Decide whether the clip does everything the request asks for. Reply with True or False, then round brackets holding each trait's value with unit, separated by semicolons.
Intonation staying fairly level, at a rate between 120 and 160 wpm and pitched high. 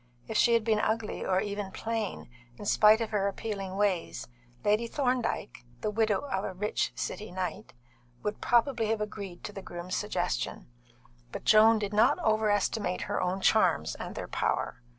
False (2.3 semitones; 170 wpm; 210 Hz)